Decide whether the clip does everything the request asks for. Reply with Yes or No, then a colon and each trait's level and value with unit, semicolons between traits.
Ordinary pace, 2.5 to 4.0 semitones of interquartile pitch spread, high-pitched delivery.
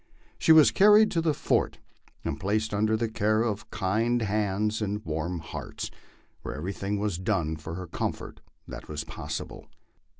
No: average, 160 wpm; average, 3.2 semitones; low, 105 Hz